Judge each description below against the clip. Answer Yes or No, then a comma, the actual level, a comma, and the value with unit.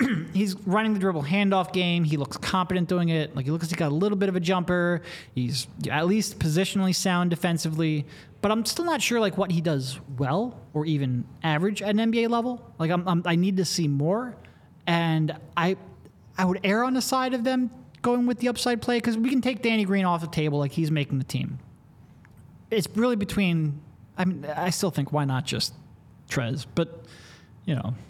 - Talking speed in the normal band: No, fast, 210 wpm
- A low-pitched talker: No, medium, 180 Hz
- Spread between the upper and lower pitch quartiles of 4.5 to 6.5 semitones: Yes, average, 5.1 semitones